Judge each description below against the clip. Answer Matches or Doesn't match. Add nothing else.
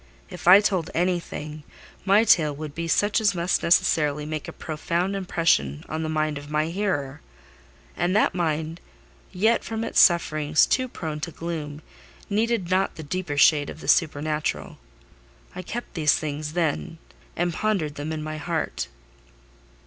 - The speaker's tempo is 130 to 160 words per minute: Matches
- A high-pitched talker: Doesn't match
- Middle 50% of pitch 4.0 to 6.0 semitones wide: Doesn't match